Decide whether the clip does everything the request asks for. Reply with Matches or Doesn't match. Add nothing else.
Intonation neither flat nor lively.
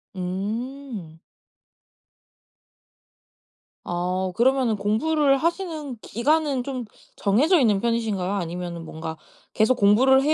Doesn't match